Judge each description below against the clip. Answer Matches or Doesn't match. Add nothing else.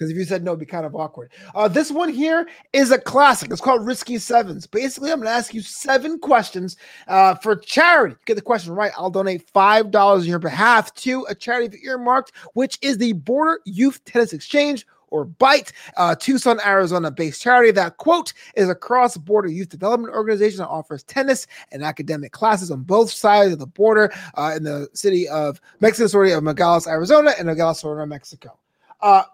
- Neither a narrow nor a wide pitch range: Doesn't match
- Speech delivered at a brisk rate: Doesn't match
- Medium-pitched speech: Doesn't match